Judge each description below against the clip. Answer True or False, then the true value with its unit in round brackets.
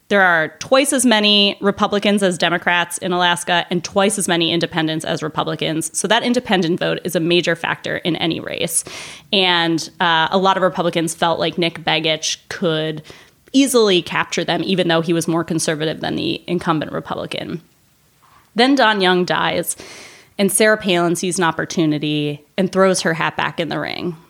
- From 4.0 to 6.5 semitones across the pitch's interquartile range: False (2.8 semitones)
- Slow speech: False (175 wpm)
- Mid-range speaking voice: True (175 Hz)